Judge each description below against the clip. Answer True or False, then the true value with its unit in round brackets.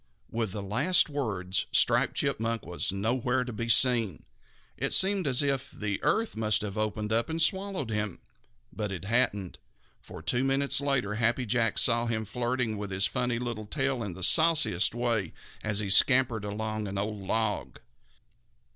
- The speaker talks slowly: False (160 wpm)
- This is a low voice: True (115 Hz)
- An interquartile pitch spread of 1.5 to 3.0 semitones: False (3.5 semitones)